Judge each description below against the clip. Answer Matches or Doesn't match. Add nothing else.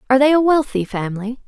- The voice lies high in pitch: Matches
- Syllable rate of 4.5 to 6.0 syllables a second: Doesn't match